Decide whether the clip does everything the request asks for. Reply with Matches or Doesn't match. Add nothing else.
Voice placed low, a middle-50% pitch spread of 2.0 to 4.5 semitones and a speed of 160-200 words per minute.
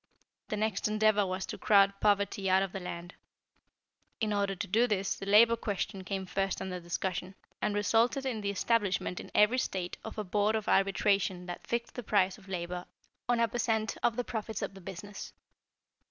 Doesn't match